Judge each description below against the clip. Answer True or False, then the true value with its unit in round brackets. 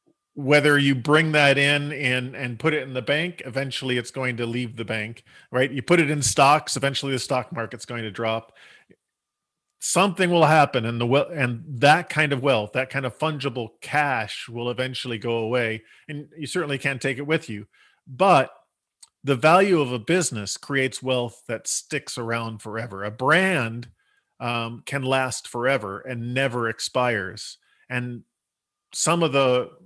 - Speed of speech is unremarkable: True (170 wpm)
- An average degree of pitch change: True (3.4 semitones)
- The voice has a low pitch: True (130 Hz)